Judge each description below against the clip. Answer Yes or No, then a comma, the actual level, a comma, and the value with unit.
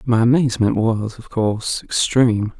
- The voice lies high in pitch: No, low, 115 Hz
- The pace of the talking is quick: No, average, 140 wpm